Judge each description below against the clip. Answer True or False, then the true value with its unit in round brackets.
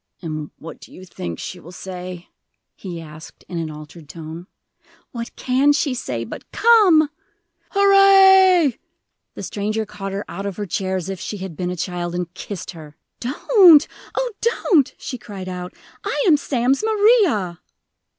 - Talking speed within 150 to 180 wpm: True (160 wpm)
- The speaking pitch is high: True (195 Hz)